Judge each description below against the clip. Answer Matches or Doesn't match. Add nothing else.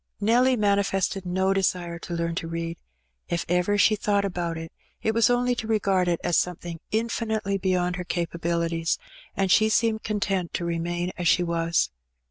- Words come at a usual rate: Matches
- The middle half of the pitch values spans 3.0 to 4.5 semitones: Matches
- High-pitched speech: Doesn't match